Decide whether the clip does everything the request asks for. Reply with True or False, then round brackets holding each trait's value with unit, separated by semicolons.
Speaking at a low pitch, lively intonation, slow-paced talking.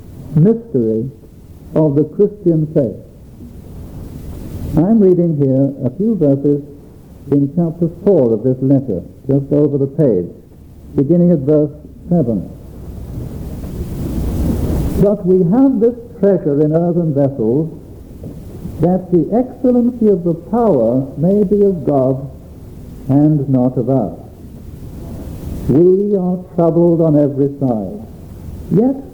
False (145 Hz; 7.6 semitones; 110 wpm)